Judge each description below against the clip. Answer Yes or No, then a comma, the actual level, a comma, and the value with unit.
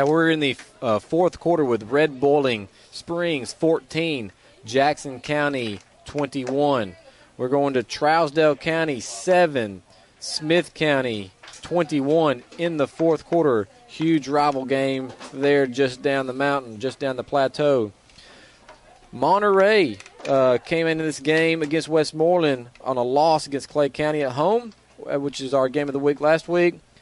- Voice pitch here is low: No, medium, 145 Hz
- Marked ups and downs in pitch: No, average, 3.5 semitones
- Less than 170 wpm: Yes, average, 140 wpm